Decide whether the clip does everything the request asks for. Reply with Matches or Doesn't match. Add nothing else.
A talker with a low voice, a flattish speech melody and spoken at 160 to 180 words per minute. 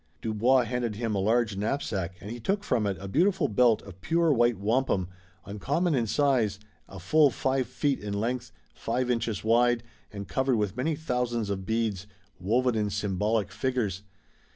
Doesn't match